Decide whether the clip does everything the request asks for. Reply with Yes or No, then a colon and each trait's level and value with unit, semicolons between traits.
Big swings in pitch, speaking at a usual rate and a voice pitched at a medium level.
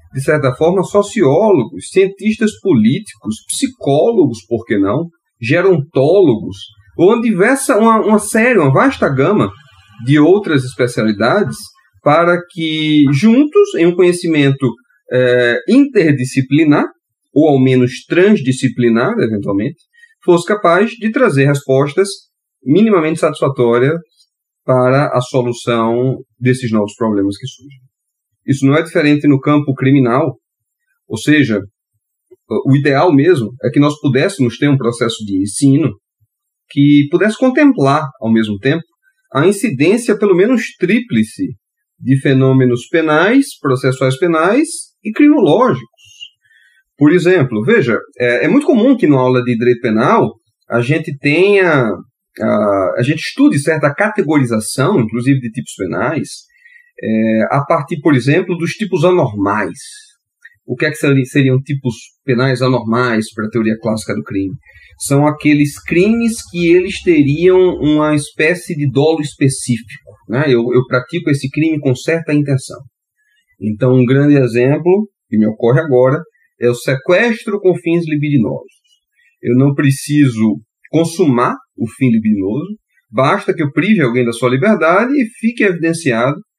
Yes: wide, 6.7 semitones; average, 130 wpm; medium, 145 Hz